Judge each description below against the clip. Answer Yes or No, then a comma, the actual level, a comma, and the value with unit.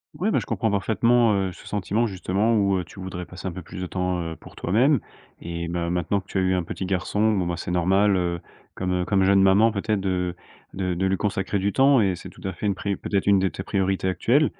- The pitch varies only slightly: Yes, narrow, 2.2 semitones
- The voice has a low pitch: Yes, very low, 95 Hz